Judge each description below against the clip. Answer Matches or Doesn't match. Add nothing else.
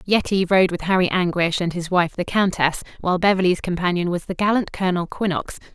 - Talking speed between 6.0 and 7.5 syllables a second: Matches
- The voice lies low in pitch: Doesn't match